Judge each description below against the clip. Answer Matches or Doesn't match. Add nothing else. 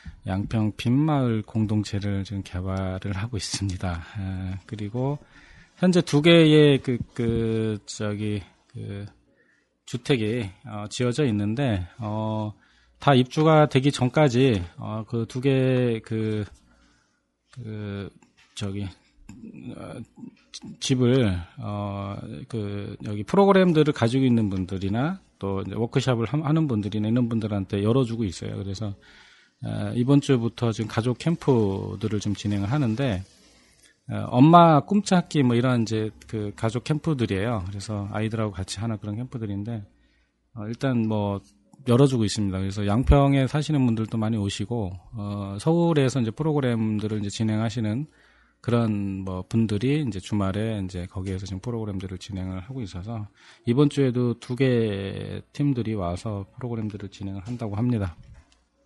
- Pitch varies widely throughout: Doesn't match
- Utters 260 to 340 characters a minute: Matches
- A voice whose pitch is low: Matches